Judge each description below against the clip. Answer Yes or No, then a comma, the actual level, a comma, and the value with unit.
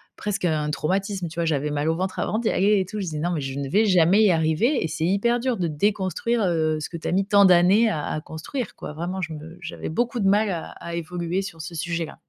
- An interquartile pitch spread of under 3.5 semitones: No, average, 4.1 semitones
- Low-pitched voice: No, medium, 175 Hz